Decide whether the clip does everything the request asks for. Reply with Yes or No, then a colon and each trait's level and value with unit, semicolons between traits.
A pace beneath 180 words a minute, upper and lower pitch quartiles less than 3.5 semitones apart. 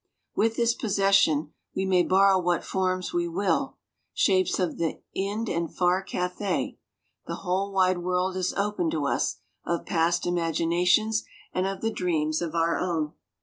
Yes: average, 155 wpm; narrow, 2.4 semitones